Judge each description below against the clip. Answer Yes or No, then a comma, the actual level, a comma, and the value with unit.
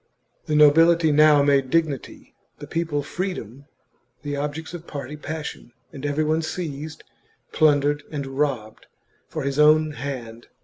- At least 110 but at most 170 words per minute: Yes, slow, 135 wpm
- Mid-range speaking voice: Yes, medium, 150 Hz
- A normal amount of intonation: No, narrow, 1.9 semitones